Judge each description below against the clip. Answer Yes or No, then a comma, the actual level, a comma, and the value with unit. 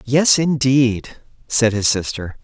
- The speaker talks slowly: Yes, slow, 125 wpm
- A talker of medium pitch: No, low, 125 Hz